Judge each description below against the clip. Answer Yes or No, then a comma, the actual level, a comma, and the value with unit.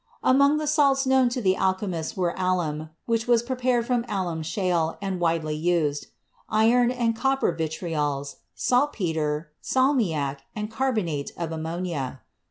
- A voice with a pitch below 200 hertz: Yes, medium, 185 Hz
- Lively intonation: Yes, wide, 7.3 semitones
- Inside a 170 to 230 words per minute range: No, slow, 135 wpm